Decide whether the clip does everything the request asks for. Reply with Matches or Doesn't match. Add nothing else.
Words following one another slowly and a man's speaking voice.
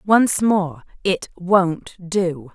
Doesn't match